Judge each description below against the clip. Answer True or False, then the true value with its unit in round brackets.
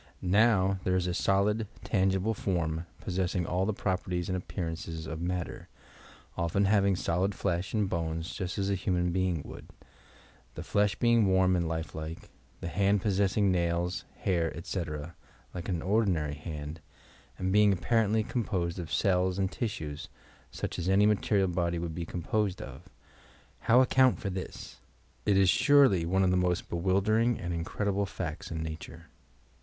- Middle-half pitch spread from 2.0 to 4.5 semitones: True (2.8 semitones)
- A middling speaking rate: True (165 wpm)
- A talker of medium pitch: False (95 Hz)